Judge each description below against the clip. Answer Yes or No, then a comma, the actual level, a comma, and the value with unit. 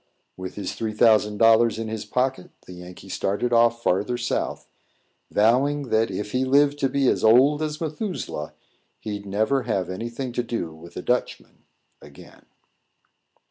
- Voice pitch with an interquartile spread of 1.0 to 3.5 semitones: No, average, 4.2 semitones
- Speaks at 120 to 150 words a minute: No, average, 160 wpm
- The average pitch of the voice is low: Yes, low, 115 Hz